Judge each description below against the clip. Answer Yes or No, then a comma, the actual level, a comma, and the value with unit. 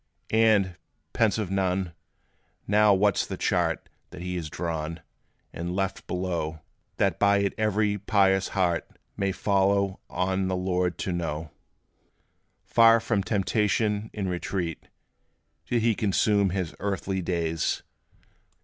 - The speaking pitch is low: Yes, very low, 95 Hz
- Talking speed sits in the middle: No, slow, 125 wpm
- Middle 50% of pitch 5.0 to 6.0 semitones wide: No, narrow, 2.5 semitones